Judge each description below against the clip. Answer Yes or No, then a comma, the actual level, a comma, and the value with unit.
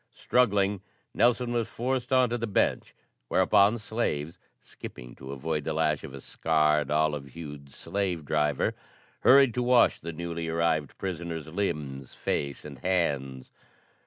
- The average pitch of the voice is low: Yes, very low, 80 Hz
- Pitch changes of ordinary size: No, wide, 6.0 semitones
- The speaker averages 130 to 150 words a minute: Yes, average, 140 wpm